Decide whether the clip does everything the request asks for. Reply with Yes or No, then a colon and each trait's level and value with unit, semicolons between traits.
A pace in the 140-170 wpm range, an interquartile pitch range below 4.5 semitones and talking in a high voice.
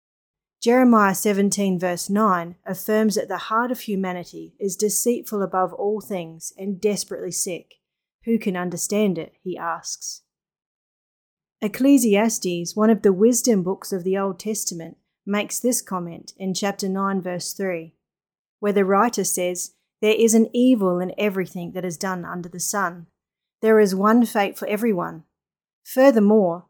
Yes: average, 145 wpm; average, 3.1 semitones; high, 195 Hz